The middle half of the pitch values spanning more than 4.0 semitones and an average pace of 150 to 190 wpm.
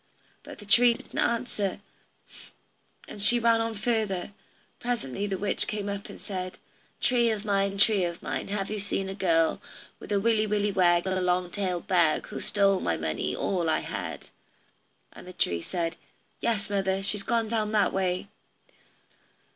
No: average, 2.7 semitones; average, 170 wpm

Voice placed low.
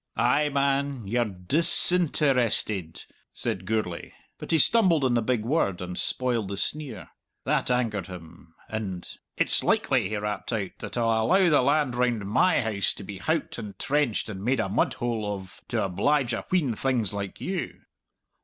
Yes: low, 115 Hz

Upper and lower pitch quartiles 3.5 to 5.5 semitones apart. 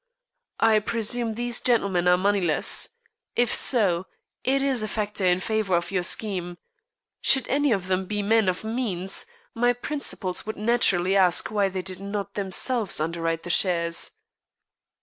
Yes: average, 3.8 semitones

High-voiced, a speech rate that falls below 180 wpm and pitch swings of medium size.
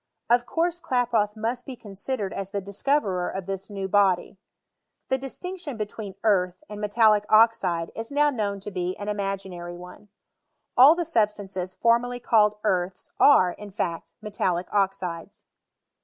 Yes: high, 205 Hz; average, 150 wpm; average, 3.8 semitones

